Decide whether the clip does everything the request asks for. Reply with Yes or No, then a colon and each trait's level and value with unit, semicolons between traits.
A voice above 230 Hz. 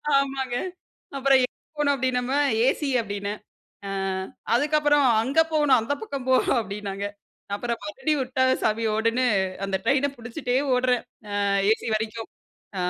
Yes: very high, 255 Hz